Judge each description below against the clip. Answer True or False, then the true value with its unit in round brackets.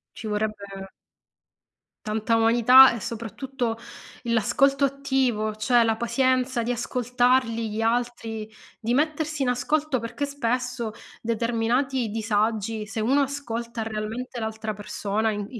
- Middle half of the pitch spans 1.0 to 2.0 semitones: False (2.7 semitones)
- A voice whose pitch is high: True (230 Hz)